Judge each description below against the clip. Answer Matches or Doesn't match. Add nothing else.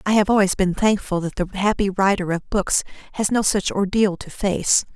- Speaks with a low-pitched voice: Doesn't match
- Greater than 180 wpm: Matches